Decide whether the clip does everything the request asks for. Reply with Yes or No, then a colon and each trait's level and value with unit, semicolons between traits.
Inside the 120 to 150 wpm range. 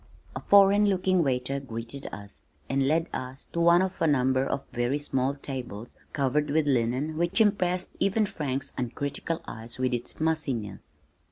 No: average, 160 wpm